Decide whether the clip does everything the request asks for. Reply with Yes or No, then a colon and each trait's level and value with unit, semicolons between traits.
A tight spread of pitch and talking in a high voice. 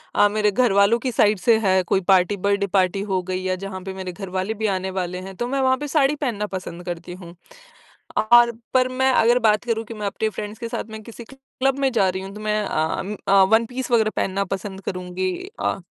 No: average, 4.0 semitones; high, 205 Hz